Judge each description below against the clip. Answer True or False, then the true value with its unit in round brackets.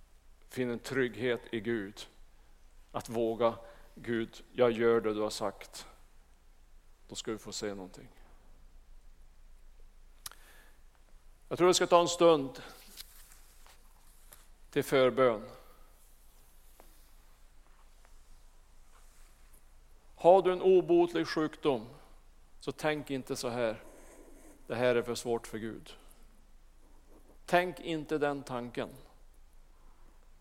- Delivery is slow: True (100 wpm)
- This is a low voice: True (115 Hz)